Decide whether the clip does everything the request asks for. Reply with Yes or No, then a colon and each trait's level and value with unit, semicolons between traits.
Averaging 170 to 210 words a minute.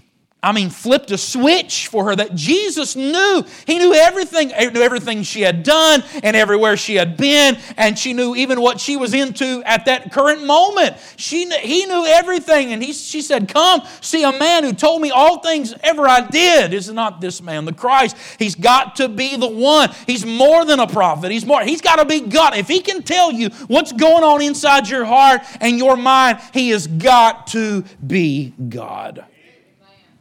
Yes: average, 195 wpm